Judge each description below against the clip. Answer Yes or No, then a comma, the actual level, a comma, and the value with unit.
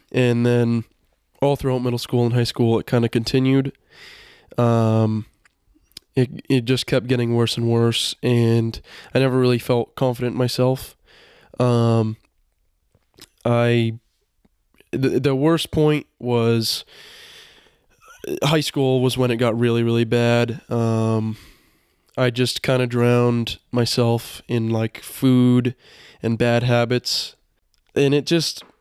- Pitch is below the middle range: Yes, low, 120 Hz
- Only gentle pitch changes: Yes, narrow, 2.0 semitones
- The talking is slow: Yes, slow, 130 wpm